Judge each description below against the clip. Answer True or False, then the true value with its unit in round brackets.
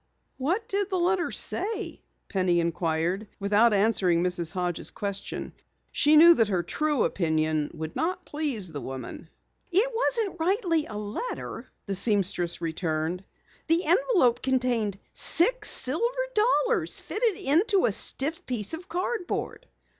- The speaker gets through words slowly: True (130 wpm)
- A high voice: True (250 Hz)